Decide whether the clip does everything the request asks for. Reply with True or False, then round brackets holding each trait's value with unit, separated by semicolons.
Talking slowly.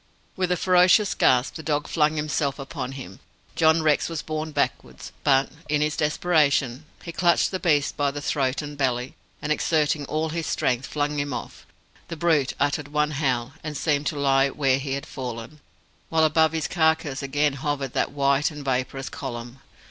False (180 wpm)